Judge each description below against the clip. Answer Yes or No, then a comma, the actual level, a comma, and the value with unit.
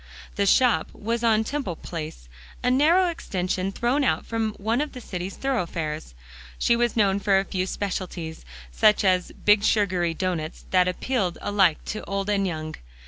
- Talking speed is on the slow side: No, average, 165 wpm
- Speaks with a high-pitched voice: Yes, high, 200 Hz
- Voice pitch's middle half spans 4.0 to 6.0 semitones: Yes, average, 4.3 semitones